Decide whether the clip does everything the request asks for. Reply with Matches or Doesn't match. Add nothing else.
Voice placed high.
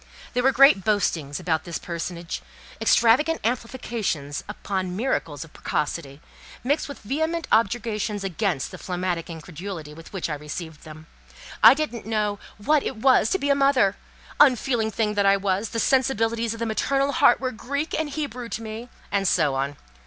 Matches